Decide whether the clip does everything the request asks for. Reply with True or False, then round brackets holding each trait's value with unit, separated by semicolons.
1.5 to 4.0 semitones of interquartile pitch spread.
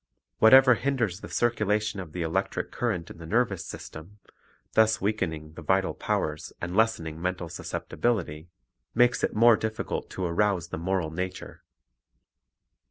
False (4.8 semitones)